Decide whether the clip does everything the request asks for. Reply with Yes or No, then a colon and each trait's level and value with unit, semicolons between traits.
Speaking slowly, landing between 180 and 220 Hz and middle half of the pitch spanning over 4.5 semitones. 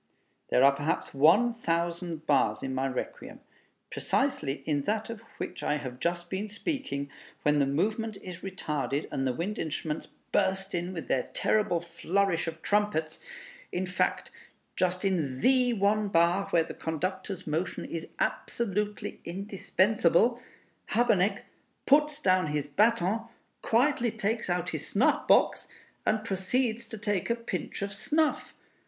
No: average, 145 wpm; medium, 185 Hz; average, 5.1 semitones